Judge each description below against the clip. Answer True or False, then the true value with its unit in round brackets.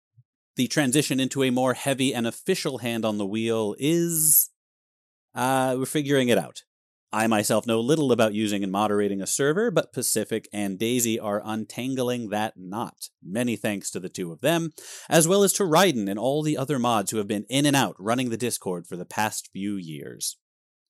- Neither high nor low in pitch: False (120 Hz)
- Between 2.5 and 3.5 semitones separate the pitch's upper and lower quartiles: False (4.3 semitones)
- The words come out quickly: False (190 wpm)